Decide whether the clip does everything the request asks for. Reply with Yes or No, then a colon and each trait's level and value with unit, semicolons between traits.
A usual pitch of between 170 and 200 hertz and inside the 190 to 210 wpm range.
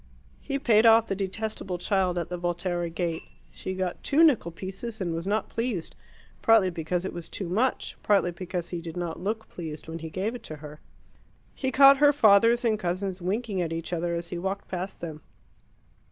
Yes: medium, 185 Hz; average, 195 wpm